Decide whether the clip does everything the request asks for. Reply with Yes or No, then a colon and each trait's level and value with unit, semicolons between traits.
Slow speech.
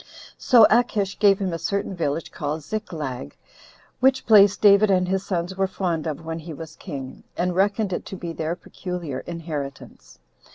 No: average, 170 wpm